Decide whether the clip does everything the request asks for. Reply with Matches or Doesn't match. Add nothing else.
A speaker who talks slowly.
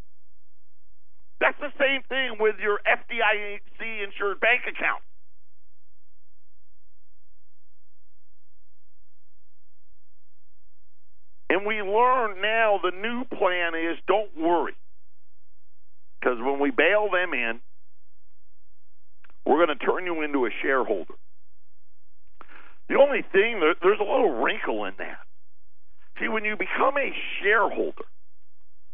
Matches